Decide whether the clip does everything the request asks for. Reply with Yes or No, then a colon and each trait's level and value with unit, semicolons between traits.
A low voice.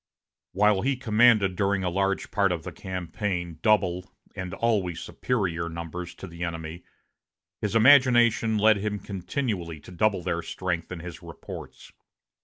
Yes: very low, 95 Hz